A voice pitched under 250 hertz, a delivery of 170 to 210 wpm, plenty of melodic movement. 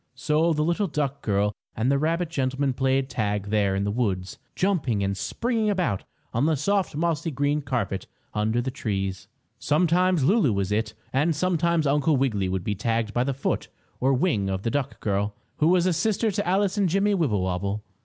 Yes: low, 135 Hz; average, 190 wpm; wide, 8.2 semitones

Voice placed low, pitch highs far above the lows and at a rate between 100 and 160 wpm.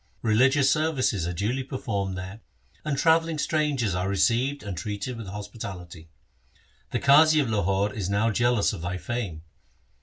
Yes: low, 110 Hz; wide, 5.8 semitones; average, 155 wpm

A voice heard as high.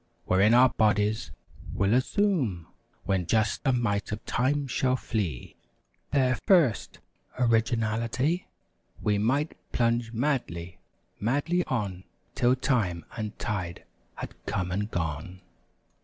No: low, 115 Hz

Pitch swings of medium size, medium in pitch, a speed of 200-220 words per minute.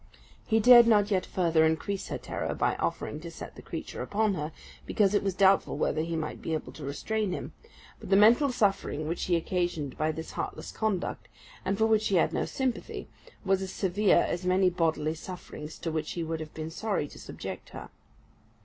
Yes: average, 4.3 semitones; medium, 180 Hz; fast, 205 wpm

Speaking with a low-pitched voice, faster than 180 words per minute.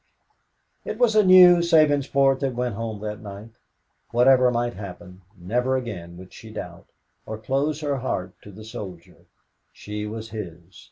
No: low, 115 Hz; average, 155 wpm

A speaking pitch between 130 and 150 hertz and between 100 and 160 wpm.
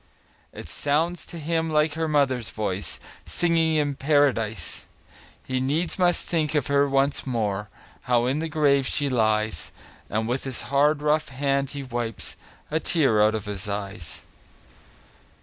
Yes: medium, 140 Hz; average, 150 wpm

